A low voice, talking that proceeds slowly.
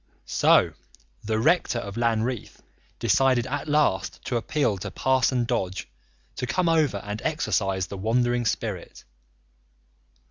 Yes: low, 120 Hz; slow, 120 wpm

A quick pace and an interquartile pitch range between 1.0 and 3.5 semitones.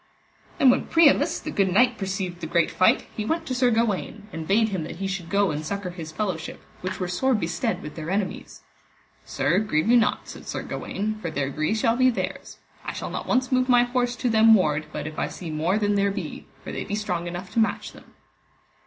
No: fast, 230 wpm; average, 4.9 semitones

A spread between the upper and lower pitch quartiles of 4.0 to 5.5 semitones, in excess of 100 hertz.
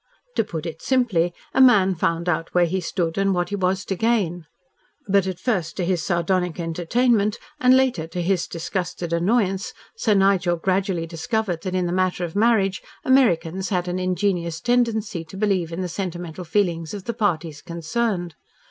No: average, 3.2 semitones; medium, 185 Hz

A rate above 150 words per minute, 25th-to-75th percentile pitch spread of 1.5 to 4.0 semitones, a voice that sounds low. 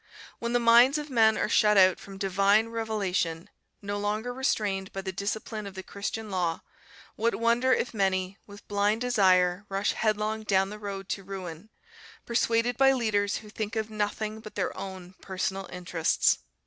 No: average, 170 wpm; narrow, 2.5 semitones; high, 205 Hz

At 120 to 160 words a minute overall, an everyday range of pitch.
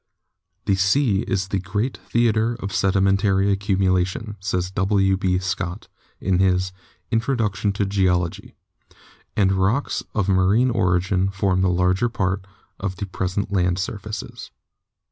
No: average, 145 wpm; narrow, 1.8 semitones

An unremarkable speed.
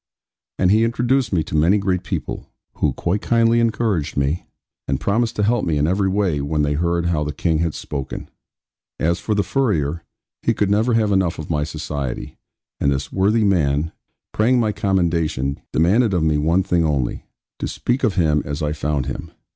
Yes: average, 190 wpm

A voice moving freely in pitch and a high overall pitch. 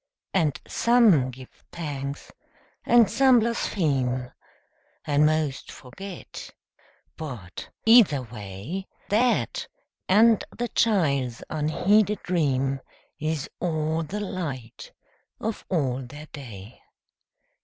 No: wide, 7.3 semitones; medium, 155 Hz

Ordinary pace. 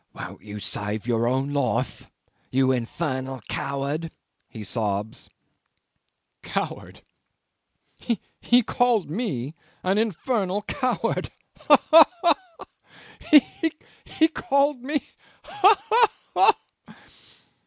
No: slow, 95 wpm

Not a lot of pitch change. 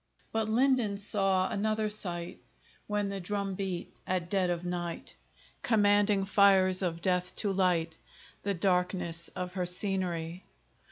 Yes: narrow, 2.3 semitones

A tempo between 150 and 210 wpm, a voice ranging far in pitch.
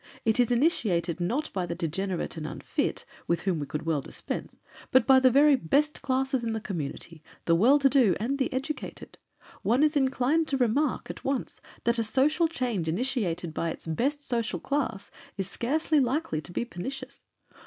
Yes: average, 185 wpm; wide, 7.5 semitones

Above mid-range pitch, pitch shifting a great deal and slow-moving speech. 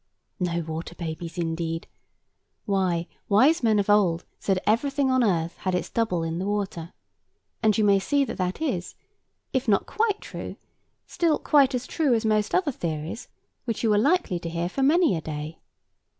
No: high, 200 Hz; wide, 7.1 semitones; average, 180 wpm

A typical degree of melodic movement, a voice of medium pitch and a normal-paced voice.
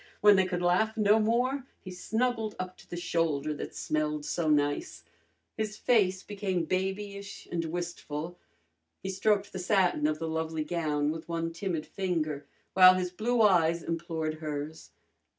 Yes: average, 4.0 semitones; medium, 175 Hz; average, 155 wpm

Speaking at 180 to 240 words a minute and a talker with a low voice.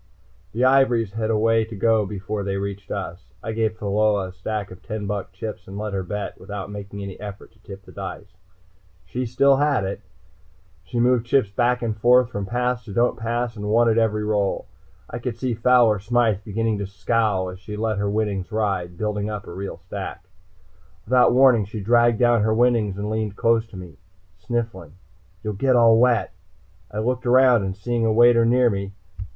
Yes: average, 200 wpm; low, 110 Hz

